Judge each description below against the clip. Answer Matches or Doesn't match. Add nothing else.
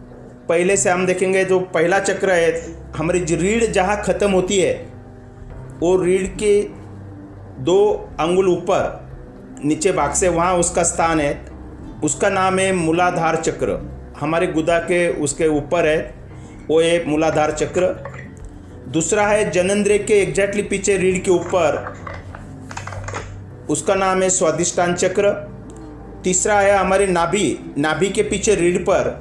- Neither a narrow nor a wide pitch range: Doesn't match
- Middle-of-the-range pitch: Matches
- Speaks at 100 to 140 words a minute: Matches